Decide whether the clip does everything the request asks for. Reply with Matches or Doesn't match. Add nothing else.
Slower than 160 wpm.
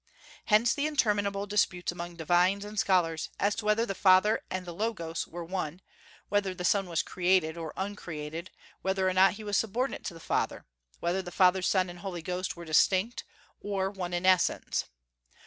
Doesn't match